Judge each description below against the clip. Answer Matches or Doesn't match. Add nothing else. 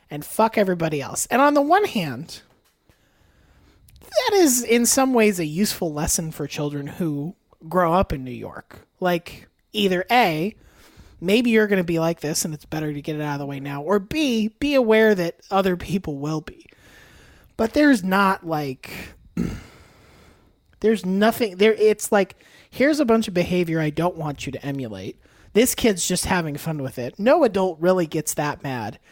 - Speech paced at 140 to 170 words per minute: Doesn't match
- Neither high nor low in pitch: Matches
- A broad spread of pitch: Matches